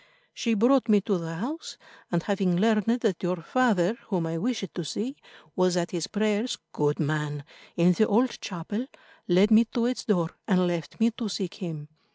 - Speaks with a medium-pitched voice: No, high, 195 Hz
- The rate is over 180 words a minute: Yes, average, 190 wpm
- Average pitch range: Yes, average, 4.8 semitones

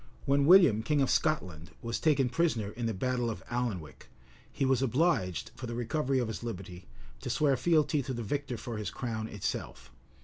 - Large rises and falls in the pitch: No, average, 4.1 semitones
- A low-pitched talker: Yes, low, 120 Hz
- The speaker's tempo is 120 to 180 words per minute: No, average, 190 wpm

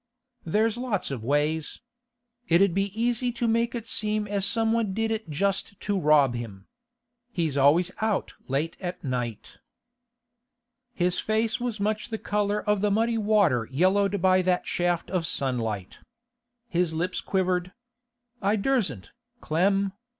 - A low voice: No, high, 190 Hz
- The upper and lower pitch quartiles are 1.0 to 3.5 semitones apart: No, average, 5.1 semitones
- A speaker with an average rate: Yes, average, 145 wpm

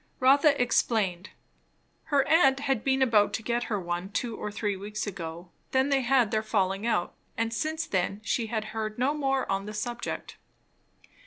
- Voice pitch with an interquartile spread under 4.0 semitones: No, average, 4.6 semitones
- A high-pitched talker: Yes, high, 225 Hz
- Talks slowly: No, average, 180 wpm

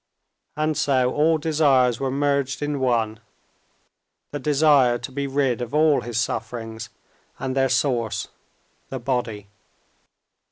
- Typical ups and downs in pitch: Yes, average, 3.1 semitones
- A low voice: Yes, low, 130 Hz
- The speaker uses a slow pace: Yes, slow, 120 wpm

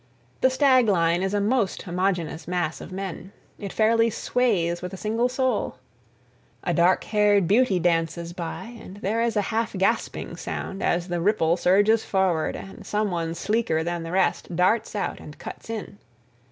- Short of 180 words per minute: Yes, average, 170 wpm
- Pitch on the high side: Yes, high, 195 Hz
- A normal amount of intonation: Yes, average, 4.0 semitones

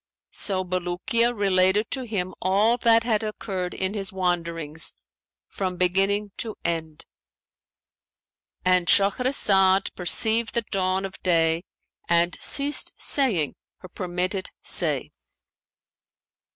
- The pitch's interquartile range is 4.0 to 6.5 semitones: No, average, 3.0 semitones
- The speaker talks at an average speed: No, slow, 100 wpm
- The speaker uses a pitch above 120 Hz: Yes, high, 190 Hz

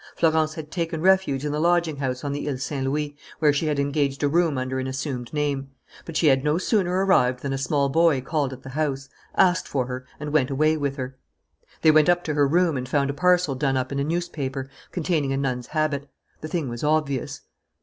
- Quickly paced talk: Yes, fast, 230 wpm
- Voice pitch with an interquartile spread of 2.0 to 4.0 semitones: Yes, average, 2.8 semitones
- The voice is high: No, medium, 145 Hz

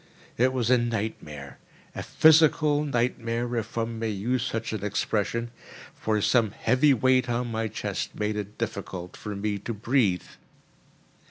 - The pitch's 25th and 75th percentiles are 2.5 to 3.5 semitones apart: Yes, average, 2.9 semitones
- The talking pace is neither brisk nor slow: Yes, average, 150 wpm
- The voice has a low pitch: Yes, low, 115 Hz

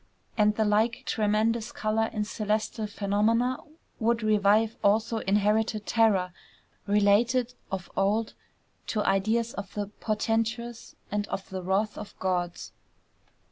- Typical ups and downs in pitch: No, narrow, 1.8 semitones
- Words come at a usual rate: No, slow, 120 wpm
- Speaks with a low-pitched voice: No, high, 215 Hz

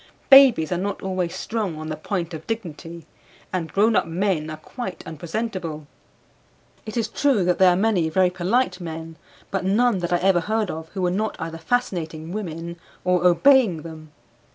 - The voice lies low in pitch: No, medium, 180 Hz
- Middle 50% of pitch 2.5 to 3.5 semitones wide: No, average, 4.3 semitones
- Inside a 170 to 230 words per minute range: Yes, average, 175 wpm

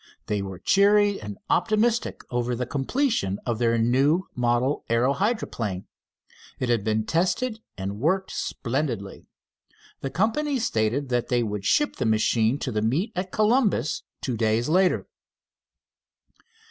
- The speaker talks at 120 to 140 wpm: Yes, slow, 135 wpm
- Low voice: Yes, low, 125 Hz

